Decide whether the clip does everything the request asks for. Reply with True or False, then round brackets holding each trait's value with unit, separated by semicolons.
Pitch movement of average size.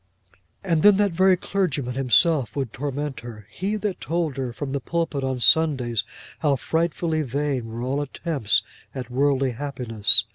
True (4.7 semitones)